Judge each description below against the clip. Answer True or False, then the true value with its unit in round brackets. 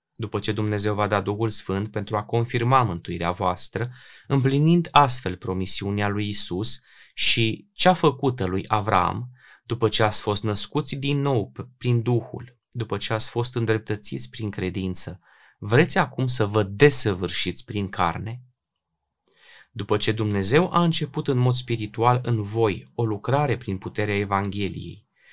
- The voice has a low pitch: True (110 Hz)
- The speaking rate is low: False (140 wpm)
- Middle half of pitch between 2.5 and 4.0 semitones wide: True (3.6 semitones)